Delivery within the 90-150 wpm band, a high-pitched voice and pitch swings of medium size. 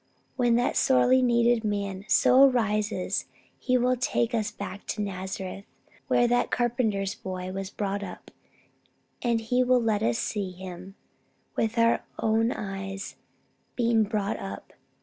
Yes: average, 140 wpm; high, 215 Hz; average, 3.6 semitones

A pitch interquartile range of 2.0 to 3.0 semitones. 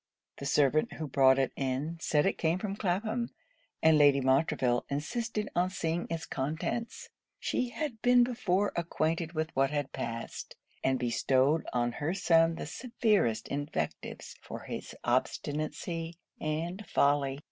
No: average, 4.9 semitones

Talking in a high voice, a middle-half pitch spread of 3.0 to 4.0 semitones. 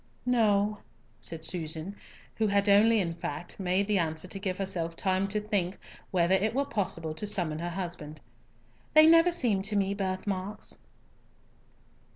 Yes: high, 195 Hz; average, 3.3 semitones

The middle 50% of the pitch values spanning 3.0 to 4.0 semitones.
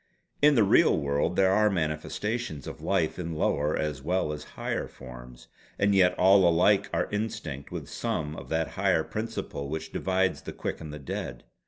No: average, 4.7 semitones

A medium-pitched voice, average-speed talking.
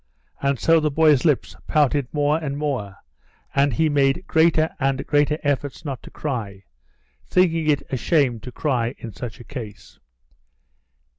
Yes: medium, 145 Hz; average, 155 wpm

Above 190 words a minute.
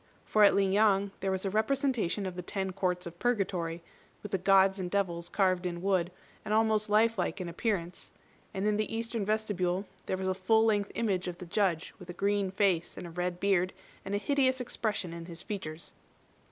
Yes: fast, 205 wpm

